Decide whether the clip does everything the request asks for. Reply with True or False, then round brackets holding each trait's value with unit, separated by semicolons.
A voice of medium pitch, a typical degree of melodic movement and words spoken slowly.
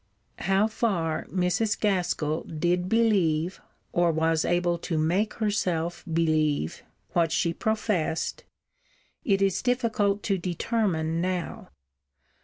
True (175 Hz; 3.8 semitones; 105 wpm)